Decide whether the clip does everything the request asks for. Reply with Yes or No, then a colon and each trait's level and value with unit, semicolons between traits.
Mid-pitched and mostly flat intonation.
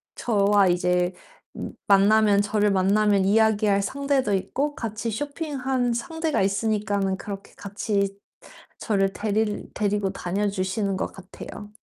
No: high, 205 Hz; narrow, 2.1 semitones